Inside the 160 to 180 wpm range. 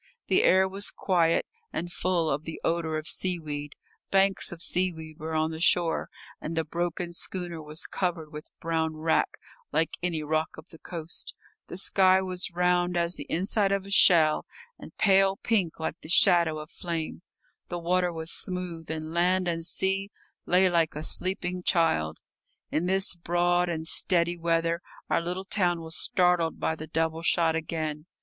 Yes: average, 170 wpm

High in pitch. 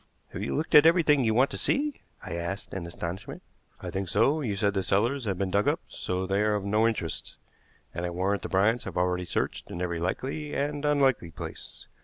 No: low, 100 Hz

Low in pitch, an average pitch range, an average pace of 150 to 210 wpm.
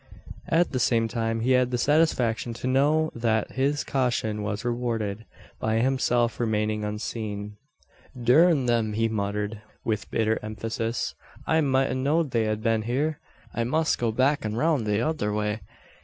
Yes: low, 115 Hz; average, 3.3 semitones; average, 160 wpm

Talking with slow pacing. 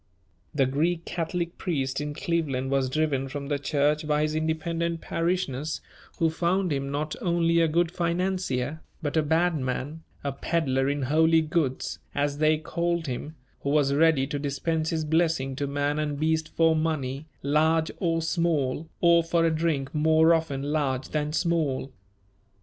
No: average, 160 wpm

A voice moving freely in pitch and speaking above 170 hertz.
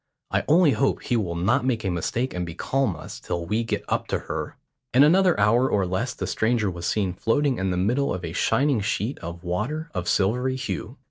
No: wide, 6.3 semitones; low, 110 Hz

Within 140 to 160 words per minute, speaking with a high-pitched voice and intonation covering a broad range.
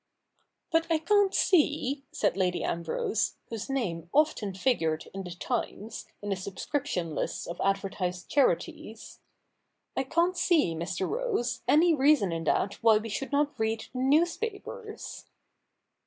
Yes: average, 150 wpm; high, 230 Hz; wide, 8.5 semitones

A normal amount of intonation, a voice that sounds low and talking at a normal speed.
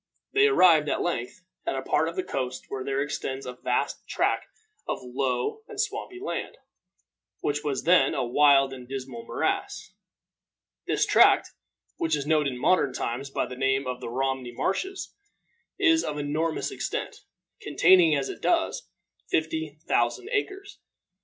No: average, 4.6 semitones; medium, 145 Hz; average, 155 wpm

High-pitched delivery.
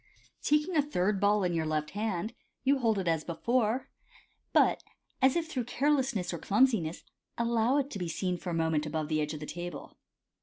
Yes: high, 200 Hz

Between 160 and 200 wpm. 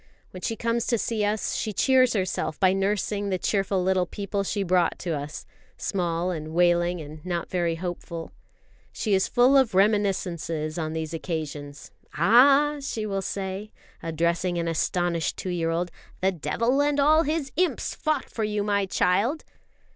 Yes: average, 165 wpm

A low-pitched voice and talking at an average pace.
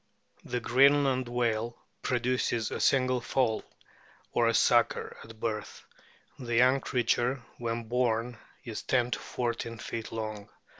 No: low, 120 Hz; slow, 130 wpm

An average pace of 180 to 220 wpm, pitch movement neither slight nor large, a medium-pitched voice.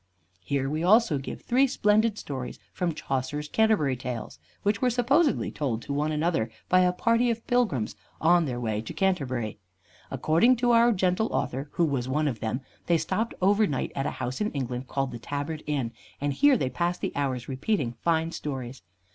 No: average, 190 wpm; wide, 8.1 semitones; medium, 150 Hz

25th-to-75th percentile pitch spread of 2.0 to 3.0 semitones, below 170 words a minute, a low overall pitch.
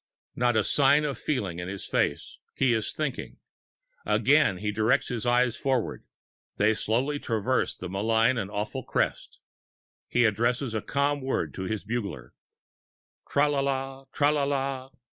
No: average, 4.2 semitones; average, 155 wpm; low, 120 Hz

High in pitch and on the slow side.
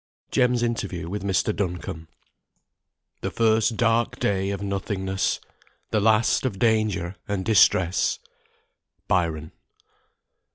No: low, 100 Hz; slow, 100 wpm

